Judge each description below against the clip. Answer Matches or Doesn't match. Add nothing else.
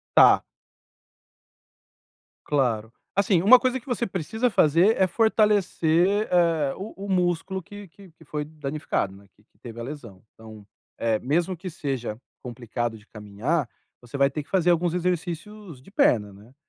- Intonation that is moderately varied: Doesn't match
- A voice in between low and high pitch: Matches